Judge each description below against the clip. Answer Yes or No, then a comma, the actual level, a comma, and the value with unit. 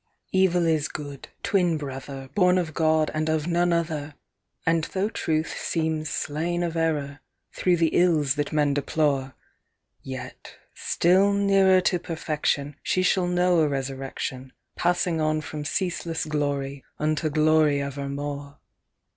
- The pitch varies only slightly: No, average, 3.3 semitones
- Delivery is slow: No, average, 145 wpm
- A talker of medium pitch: Yes, medium, 155 Hz